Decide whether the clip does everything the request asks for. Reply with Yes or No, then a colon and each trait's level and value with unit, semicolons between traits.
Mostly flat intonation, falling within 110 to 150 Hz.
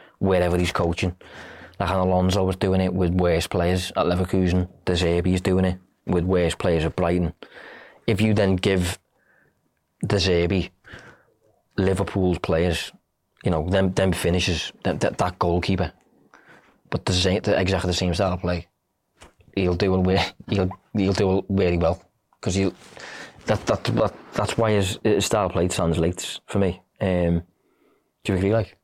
No: narrow, 1.5 semitones; very low, 95 Hz